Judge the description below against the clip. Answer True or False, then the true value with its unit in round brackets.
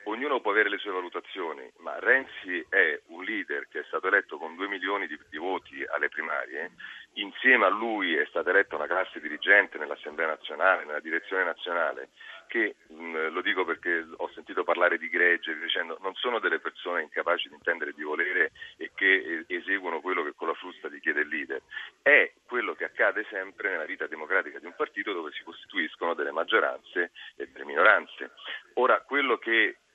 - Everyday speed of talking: False (180 wpm)